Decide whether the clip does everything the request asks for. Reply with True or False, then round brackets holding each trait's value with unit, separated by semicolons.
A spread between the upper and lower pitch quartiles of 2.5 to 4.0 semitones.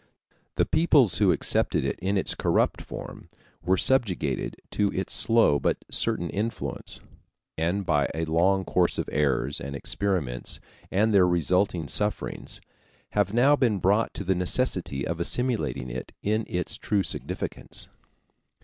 False (4.4 semitones)